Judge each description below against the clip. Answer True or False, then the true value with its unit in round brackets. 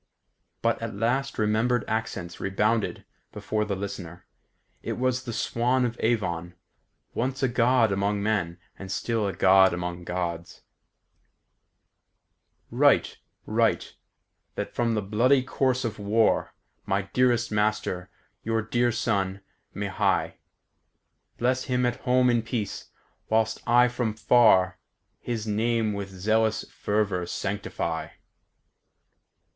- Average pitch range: True (3.6 semitones)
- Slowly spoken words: True (120 wpm)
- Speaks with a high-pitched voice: False (110 Hz)